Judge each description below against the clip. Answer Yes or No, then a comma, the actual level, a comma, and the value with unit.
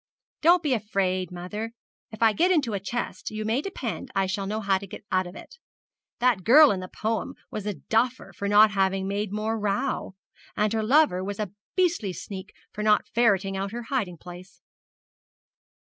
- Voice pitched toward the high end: Yes, high, 210 Hz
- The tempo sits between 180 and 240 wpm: Yes, average, 190 wpm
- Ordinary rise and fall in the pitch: Yes, average, 3.4 semitones